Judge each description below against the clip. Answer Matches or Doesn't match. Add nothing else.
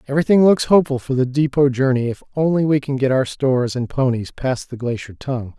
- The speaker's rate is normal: Doesn't match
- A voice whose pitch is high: Doesn't match